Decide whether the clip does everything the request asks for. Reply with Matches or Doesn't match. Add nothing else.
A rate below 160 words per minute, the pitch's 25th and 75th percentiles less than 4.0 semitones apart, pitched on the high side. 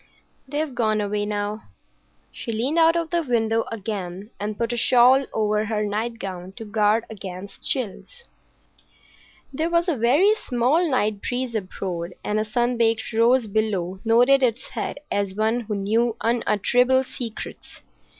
Matches